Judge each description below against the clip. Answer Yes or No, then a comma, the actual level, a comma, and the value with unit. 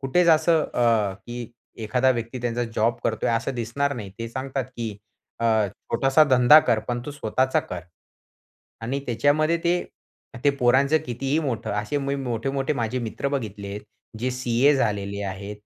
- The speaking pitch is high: No, low, 125 Hz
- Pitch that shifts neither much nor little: Yes, average, 3.4 semitones